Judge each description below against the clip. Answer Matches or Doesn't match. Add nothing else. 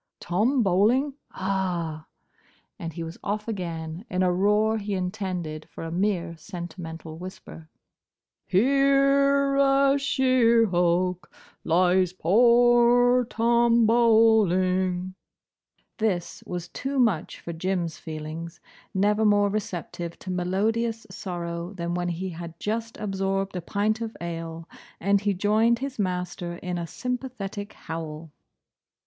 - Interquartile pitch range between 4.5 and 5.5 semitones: Matches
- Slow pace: Matches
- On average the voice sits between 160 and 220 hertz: Matches